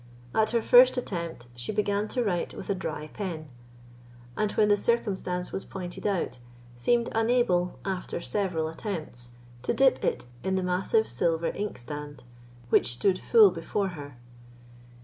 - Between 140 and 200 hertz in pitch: Yes, medium, 185 Hz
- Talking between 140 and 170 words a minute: Yes, average, 150 wpm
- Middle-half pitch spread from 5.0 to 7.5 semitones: No, average, 4.5 semitones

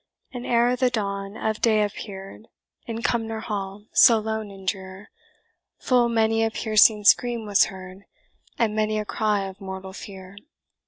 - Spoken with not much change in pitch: Yes, narrow, 2.3 semitones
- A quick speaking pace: No, average, 155 wpm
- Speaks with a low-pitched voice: No, high, 215 Hz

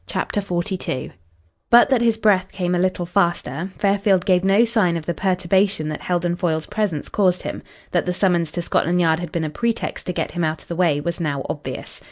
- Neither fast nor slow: No, fast, 215 wpm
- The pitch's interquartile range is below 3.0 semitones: Yes, narrow, 2.6 semitones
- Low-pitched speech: No, medium, 180 Hz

